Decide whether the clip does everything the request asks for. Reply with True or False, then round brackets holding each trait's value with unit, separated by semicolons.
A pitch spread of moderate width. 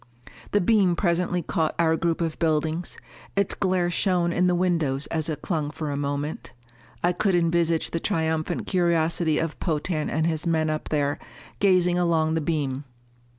False (2.0 semitones)